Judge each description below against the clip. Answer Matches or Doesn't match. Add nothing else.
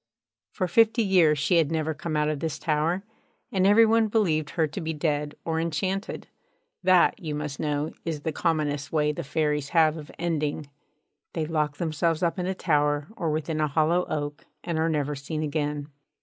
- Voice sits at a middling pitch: Matches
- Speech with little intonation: Matches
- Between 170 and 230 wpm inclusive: Matches